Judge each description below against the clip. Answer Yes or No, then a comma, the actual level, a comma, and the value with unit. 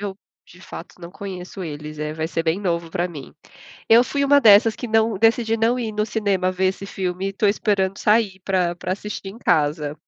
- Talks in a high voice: Yes, high, 195 Hz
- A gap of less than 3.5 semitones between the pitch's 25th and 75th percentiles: No, average, 3.8 semitones